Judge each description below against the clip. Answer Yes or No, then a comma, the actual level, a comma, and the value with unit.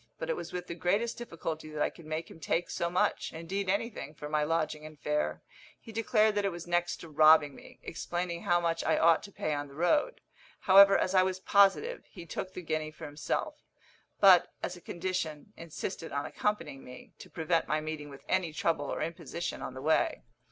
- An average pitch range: Yes, average, 3.3 semitones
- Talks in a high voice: No, medium, 170 Hz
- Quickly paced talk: Yes, fast, 210 wpm